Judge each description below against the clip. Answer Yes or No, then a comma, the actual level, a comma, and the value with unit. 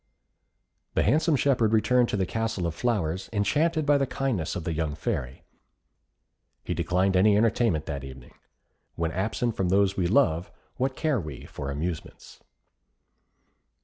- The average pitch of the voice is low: Yes, low, 100 Hz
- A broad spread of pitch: Yes, wide, 6.8 semitones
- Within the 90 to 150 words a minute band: Yes, average, 145 wpm